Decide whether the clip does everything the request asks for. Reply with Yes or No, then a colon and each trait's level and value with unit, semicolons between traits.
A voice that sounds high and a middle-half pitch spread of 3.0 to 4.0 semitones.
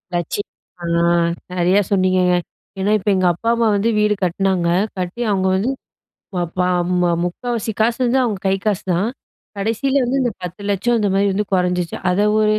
Yes: high, 200 Hz; average, 3.5 semitones